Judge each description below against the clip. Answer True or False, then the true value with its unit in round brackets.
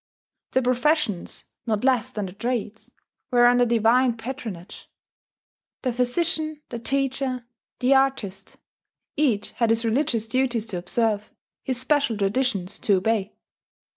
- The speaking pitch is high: True (240 Hz)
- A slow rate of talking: True (125 wpm)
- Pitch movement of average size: True (3.4 semitones)